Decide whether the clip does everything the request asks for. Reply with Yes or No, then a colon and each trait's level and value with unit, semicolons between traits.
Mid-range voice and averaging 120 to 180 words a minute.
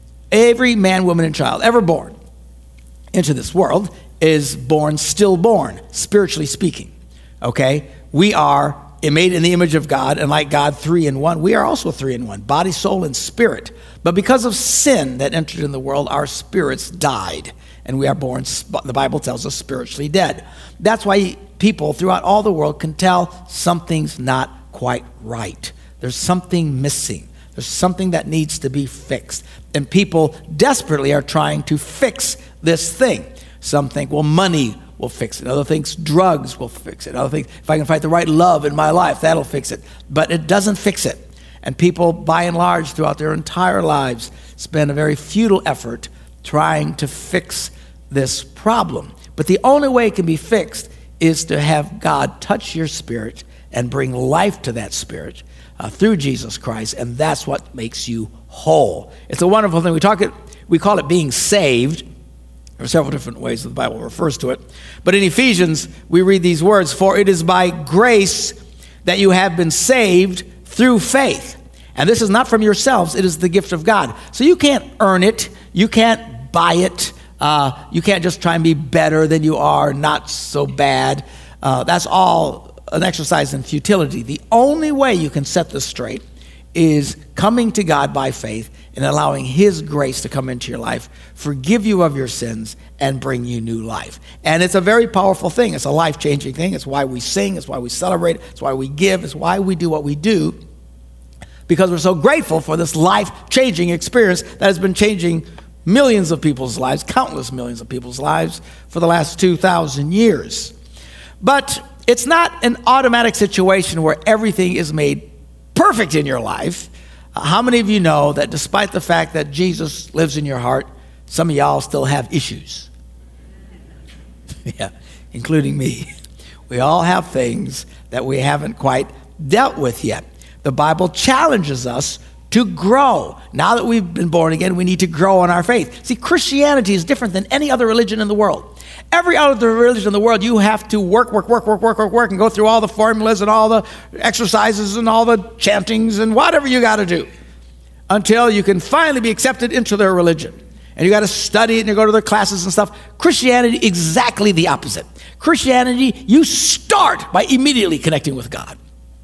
No: medium, 170 Hz; average, 190 wpm